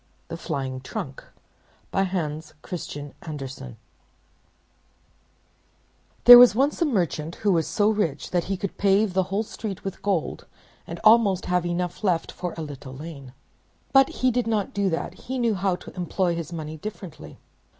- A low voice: No, medium, 180 Hz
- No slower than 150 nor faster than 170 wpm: Yes, average, 160 wpm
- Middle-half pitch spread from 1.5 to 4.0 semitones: No, average, 4.7 semitones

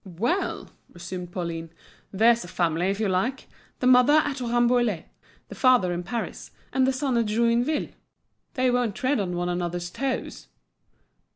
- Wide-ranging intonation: Yes, wide, 6.2 semitones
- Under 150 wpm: No, average, 155 wpm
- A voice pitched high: Yes, high, 230 Hz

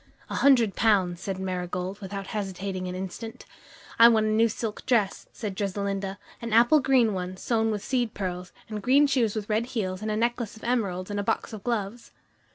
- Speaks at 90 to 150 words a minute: No, average, 195 wpm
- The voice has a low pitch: No, high, 210 Hz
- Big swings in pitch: No, average, 3.2 semitones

